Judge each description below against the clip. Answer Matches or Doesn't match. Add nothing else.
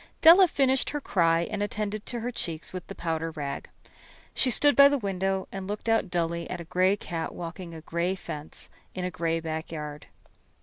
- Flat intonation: Doesn't match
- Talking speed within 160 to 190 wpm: Matches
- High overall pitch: Doesn't match